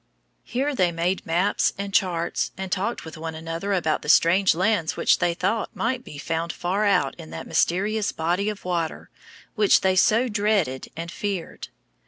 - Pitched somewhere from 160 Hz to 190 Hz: Yes, medium, 185 Hz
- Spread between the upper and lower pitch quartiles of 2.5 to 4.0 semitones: Yes, average, 3.6 semitones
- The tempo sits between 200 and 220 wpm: No, average, 175 wpm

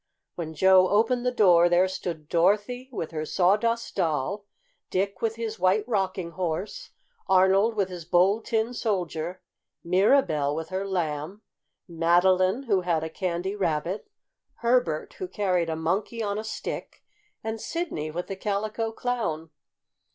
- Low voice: No, high, 190 Hz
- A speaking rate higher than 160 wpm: No, average, 145 wpm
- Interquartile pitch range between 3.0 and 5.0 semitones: Yes, average, 4.2 semitones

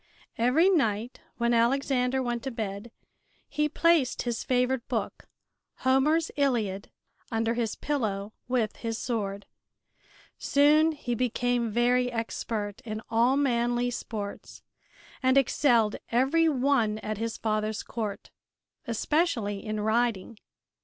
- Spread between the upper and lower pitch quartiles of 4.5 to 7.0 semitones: No, average, 3.4 semitones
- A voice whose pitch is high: Yes, high, 240 Hz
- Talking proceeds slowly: Yes, slow, 115 wpm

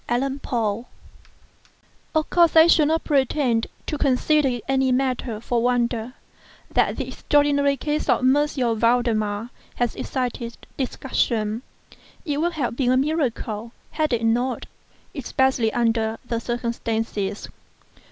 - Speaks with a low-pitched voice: No, very high, 250 Hz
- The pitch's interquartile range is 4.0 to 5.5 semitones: No, average, 3.4 semitones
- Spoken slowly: Yes, slow, 120 wpm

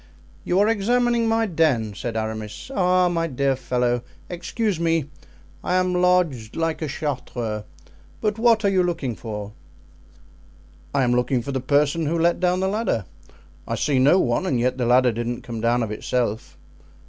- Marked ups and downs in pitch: Yes, wide, 7.0 semitones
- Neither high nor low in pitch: Yes, medium, 145 Hz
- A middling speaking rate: Yes, average, 170 wpm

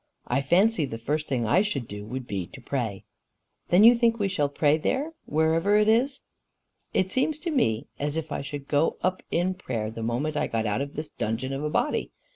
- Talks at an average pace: No, fast, 220 wpm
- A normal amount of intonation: No, wide, 7.5 semitones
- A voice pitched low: No, medium, 150 Hz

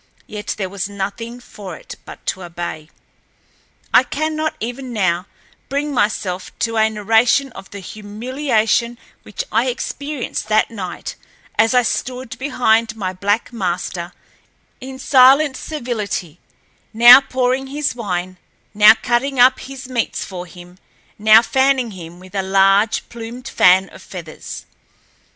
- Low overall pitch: No, high, 225 Hz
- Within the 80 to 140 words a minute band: Yes, slow, 135 wpm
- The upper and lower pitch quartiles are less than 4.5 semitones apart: No, average, 4.8 semitones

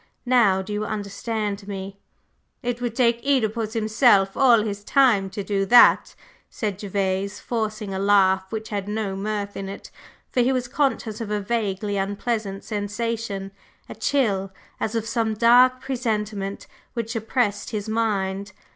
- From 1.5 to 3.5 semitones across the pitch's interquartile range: Yes, average, 2.8 semitones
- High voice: Yes, high, 215 Hz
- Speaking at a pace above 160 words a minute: No, average, 150 wpm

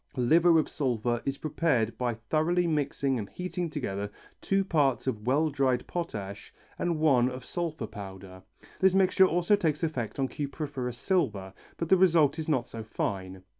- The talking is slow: No, average, 165 wpm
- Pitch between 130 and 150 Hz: Yes, medium, 140 Hz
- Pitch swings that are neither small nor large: No, wide, 6.1 semitones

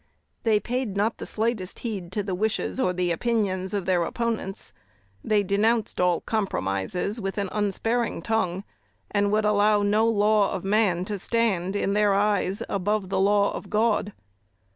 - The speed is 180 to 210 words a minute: No, average, 165 wpm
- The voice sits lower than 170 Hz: No, high, 205 Hz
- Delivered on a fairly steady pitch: Yes, narrow, 2.3 semitones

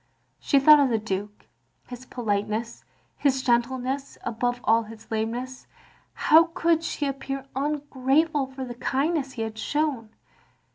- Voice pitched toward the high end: Yes, very high, 260 Hz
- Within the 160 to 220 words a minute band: No, slow, 135 wpm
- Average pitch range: Yes, average, 3.7 semitones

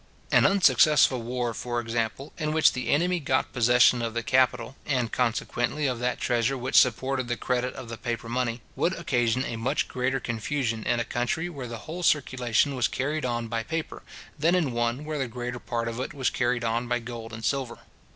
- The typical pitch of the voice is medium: No, low, 125 Hz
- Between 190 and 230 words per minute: Yes, average, 200 wpm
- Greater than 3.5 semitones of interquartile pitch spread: No, narrow, 2.5 semitones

